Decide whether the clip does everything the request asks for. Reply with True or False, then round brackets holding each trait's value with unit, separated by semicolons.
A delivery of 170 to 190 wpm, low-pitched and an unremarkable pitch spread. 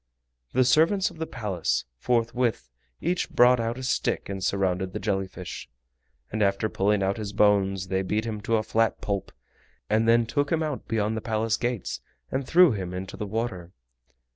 True (185 wpm; 110 Hz; 3.9 semitones)